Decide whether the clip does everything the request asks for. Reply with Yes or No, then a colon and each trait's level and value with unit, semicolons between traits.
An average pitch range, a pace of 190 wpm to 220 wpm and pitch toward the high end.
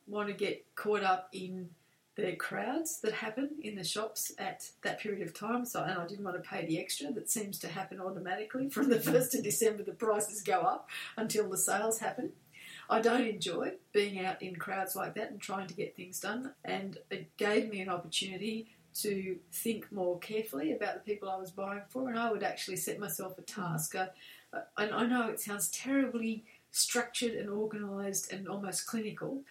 Yes: average, 3.0 semitones; average, 200 wpm; high, 205 Hz